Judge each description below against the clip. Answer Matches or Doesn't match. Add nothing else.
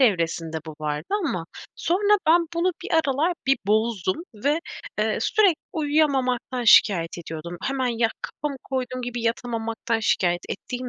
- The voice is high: Matches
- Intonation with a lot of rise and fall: Matches